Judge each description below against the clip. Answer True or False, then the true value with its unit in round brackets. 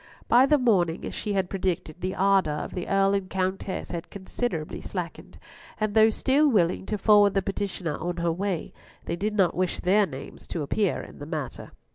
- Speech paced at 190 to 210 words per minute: True (195 wpm)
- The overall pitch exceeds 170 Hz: True (190 Hz)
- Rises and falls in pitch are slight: False (3.0 semitones)